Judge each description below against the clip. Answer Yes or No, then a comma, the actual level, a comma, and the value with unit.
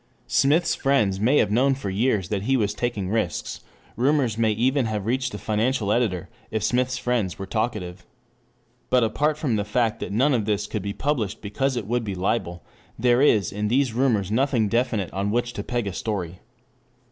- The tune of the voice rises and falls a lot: No, average, 3.8 semitones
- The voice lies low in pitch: Yes, low, 110 Hz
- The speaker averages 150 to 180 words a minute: No, average, 195 wpm